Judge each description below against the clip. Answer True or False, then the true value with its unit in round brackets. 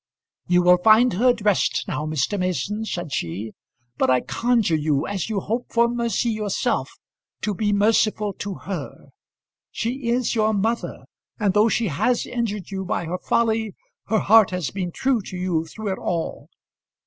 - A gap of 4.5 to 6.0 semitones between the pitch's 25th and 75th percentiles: False (4.0 semitones)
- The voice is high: True (205 Hz)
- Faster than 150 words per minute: True (170 wpm)